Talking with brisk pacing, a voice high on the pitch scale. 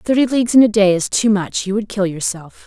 Yes: fast, 270 wpm; high, 205 Hz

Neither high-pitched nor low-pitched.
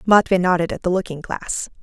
Yes: medium, 180 Hz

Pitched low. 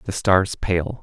Yes: very low, 90 Hz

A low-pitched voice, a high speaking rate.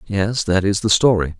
Yes: low, 100 Hz; fast, 215 wpm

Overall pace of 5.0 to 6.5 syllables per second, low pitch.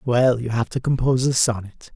Yes: 5.5 syllables/s; low, 120 Hz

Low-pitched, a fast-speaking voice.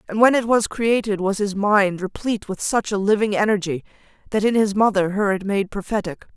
No: high, 205 Hz; fast, 210 wpm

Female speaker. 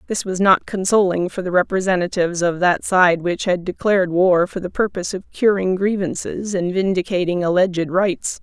Yes: female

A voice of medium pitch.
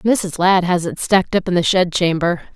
Yes: medium, 180 Hz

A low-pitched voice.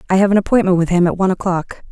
No: medium, 185 Hz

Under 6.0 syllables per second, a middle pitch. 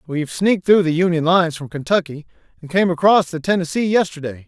No: 6.3 syllables/s; medium, 170 Hz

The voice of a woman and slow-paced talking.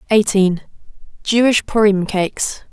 Yes: female; slow, 65 wpm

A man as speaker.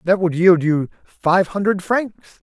Yes: male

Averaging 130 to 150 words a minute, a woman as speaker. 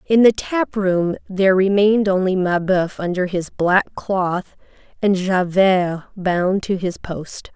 Yes: average, 145 wpm; female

